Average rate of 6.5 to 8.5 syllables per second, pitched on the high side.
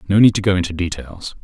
No: 6.6 syllables/s; very low, 95 Hz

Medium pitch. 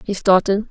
No: high, 195 Hz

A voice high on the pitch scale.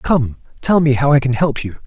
No: low, 135 Hz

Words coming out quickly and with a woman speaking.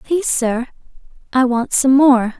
No: average, 150 wpm; female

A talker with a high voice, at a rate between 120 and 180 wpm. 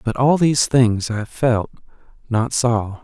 No: low, 120 Hz; average, 140 wpm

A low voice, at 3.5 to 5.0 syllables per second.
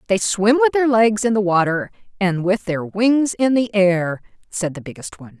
No: high, 200 Hz; 4.9 syllables/s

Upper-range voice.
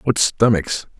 No: low, 105 Hz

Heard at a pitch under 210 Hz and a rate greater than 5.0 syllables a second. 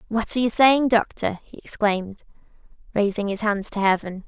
No: high, 215 Hz; 5.4 syllables/s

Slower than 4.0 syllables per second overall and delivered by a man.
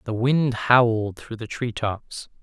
Yes: 3.7 syllables/s; male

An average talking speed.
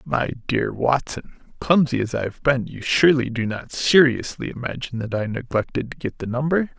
Yes: average, 185 wpm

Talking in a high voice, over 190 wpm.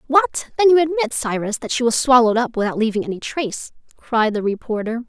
Yes: high, 240 Hz; average, 200 wpm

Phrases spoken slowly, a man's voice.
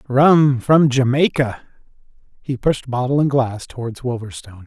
Yes: slow, 130 wpm; male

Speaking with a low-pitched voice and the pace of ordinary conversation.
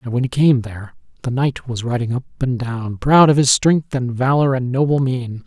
No: low, 130 Hz; fast, 230 wpm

